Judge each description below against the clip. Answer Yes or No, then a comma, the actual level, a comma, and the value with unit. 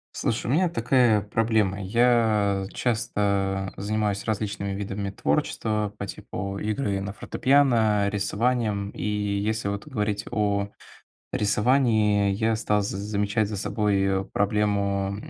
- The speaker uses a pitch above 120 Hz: No, low, 105 Hz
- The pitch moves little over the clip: Yes, narrow, 1.8 semitones